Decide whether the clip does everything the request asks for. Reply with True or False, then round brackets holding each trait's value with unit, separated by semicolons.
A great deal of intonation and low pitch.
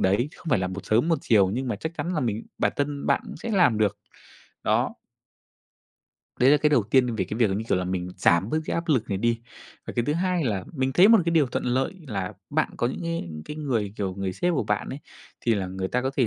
True (6.8 semitones; 120 Hz)